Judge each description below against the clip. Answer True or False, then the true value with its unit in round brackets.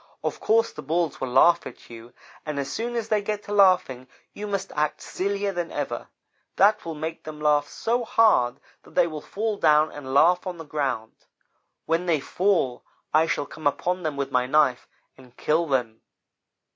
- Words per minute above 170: True (190 wpm)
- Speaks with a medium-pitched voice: True (155 Hz)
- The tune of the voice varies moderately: False (5.8 semitones)